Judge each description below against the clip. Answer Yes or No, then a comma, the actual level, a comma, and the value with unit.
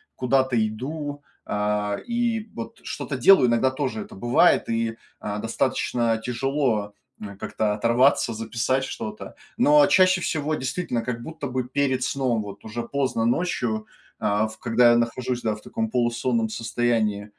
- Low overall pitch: Yes, low, 120 Hz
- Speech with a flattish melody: No, average, 3.3 semitones